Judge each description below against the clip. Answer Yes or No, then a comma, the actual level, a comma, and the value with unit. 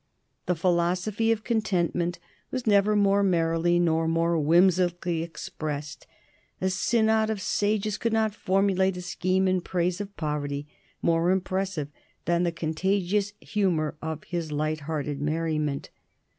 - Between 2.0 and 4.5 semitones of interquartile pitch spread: Yes, average, 3.4 semitones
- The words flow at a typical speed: No, slow, 130 wpm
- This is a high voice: No, medium, 175 Hz